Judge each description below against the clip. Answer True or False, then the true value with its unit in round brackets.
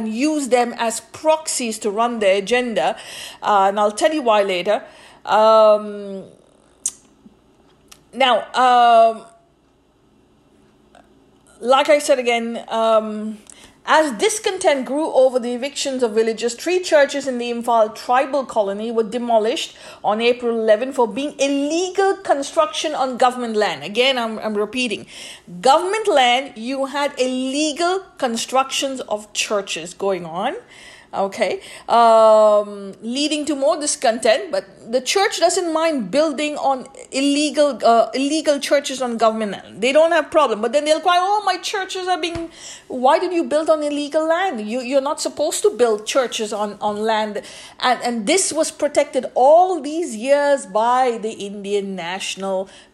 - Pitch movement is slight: False (5.5 semitones)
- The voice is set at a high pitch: True (255 Hz)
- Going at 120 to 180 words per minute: True (140 wpm)